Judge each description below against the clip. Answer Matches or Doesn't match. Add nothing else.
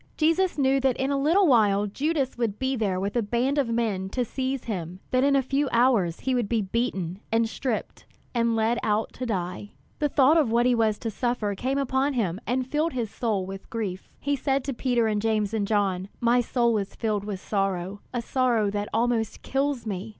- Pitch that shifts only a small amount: Doesn't match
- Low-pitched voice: Doesn't match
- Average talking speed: Doesn't match